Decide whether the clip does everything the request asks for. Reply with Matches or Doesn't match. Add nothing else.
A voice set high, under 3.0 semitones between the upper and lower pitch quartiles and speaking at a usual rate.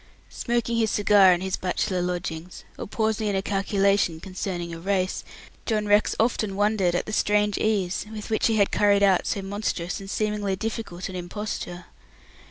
Matches